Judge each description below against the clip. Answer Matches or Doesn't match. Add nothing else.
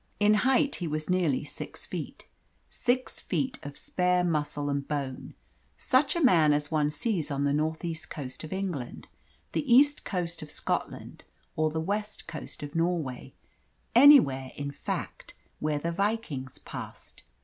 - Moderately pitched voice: Matches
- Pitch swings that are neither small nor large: Doesn't match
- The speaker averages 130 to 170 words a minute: Matches